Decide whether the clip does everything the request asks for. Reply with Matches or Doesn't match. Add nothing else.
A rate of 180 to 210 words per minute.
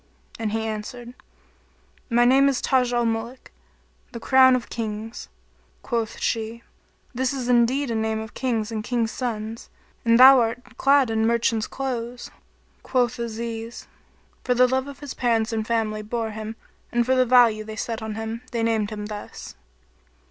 Doesn't match